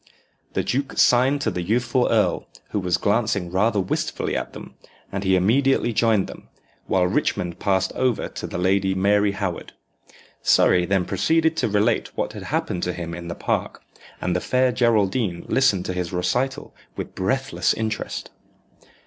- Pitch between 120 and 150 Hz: No, low, 100 Hz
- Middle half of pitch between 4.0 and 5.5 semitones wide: Yes, average, 4.9 semitones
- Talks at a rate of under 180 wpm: Yes, average, 165 wpm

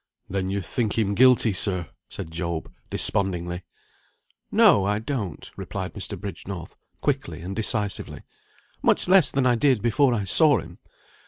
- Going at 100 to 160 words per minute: Yes, average, 145 wpm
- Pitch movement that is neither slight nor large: Yes, average, 4.5 semitones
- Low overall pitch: Yes, low, 100 Hz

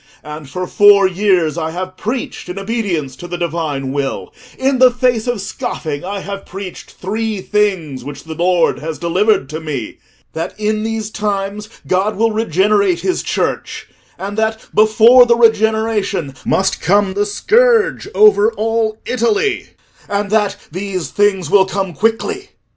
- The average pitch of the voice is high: Yes, high, 200 Hz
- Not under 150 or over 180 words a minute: Yes, average, 155 wpm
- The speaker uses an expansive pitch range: No, average, 3.9 semitones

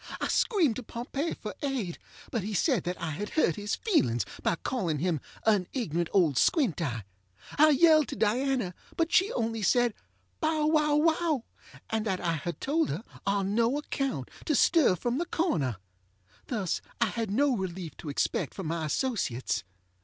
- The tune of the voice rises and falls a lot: Yes, wide, 9.0 semitones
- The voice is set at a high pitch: Yes, high, 215 Hz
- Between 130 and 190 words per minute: Yes, average, 175 wpm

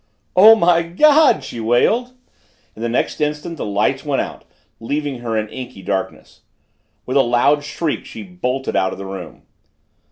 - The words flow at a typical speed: Yes, average, 165 wpm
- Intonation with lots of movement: Yes, wide, 7.0 semitones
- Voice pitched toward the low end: Yes, low, 130 Hz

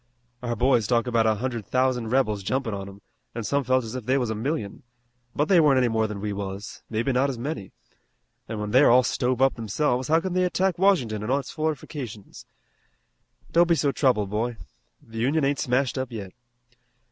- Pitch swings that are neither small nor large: Yes, average, 4.0 semitones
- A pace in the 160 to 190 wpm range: No, fast, 205 wpm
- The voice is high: No, low, 125 Hz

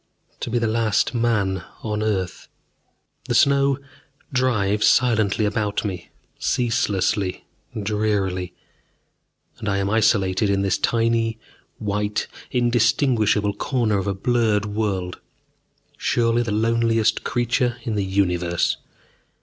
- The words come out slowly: Yes, slow, 110 wpm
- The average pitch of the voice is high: No, low, 110 Hz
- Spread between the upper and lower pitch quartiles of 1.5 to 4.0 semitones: Yes, average, 2.8 semitones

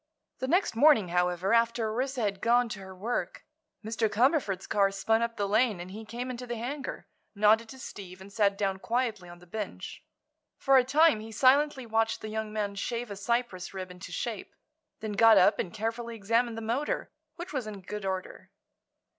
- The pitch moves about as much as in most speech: Yes, average, 3.3 semitones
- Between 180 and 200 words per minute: Yes, average, 195 wpm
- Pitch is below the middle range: No, high, 220 Hz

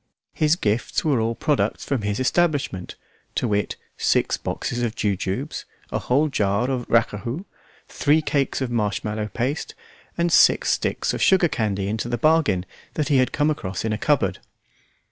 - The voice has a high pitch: No, low, 120 Hz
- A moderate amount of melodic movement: No, wide, 5.8 semitones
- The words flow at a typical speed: Yes, average, 165 wpm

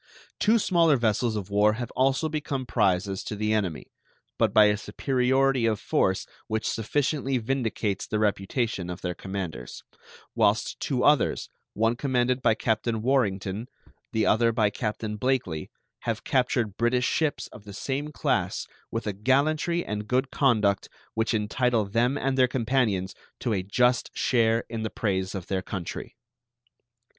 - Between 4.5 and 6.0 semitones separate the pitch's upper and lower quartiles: No, average, 3.9 semitones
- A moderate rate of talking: Yes, average, 150 wpm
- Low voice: Yes, low, 115 Hz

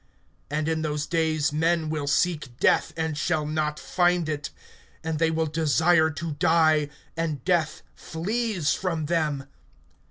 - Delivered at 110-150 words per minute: Yes, average, 140 wpm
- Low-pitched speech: No, medium, 160 Hz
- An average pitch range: No, narrow, 1.7 semitones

